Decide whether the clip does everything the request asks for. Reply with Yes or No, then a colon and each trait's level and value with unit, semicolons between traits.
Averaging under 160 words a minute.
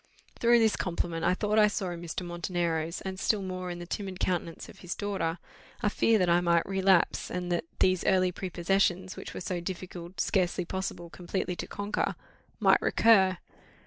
No: average, 180 wpm